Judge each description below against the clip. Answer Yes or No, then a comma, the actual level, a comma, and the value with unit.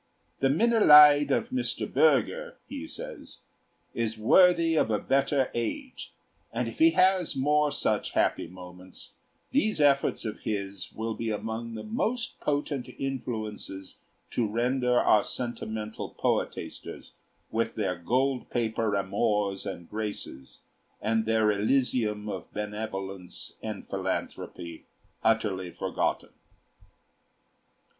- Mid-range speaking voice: No, low, 115 Hz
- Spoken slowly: Yes, slow, 115 wpm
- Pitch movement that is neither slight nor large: No, wide, 5.7 semitones